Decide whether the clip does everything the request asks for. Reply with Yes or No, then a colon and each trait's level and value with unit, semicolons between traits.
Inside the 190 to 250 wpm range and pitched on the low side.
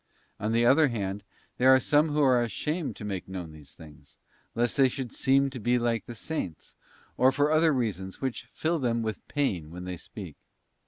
Yes: average, 200 wpm; low, 120 Hz